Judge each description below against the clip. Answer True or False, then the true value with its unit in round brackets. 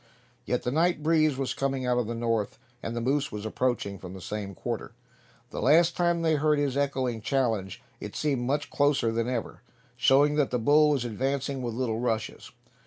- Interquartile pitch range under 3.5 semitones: False (4.0 semitones)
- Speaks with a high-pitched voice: False (130 Hz)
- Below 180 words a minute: False (195 wpm)